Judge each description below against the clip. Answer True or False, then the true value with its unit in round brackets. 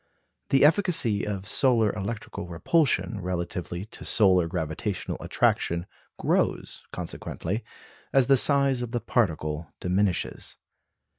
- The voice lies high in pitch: False (105 Hz)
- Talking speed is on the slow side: True (105 wpm)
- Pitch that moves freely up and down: True (5.7 semitones)